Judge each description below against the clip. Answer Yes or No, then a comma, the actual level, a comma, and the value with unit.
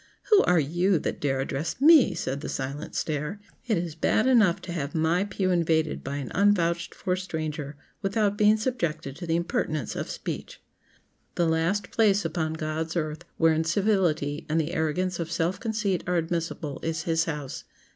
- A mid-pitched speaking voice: Yes, medium, 165 Hz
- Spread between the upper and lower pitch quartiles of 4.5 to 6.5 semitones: No, average, 3.4 semitones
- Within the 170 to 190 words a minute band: Yes, average, 175 wpm